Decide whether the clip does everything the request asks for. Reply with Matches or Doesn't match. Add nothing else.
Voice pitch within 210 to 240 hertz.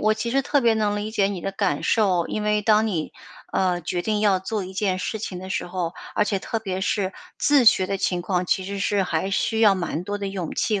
Doesn't match